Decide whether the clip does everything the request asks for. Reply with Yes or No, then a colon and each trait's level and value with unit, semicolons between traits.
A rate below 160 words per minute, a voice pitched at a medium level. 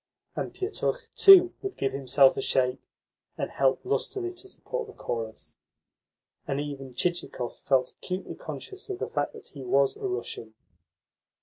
Yes: average, 150 wpm; medium, 145 Hz